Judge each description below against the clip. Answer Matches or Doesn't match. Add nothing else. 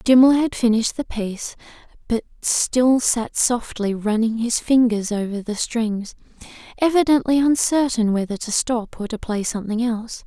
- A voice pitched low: Doesn't match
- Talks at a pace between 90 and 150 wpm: Matches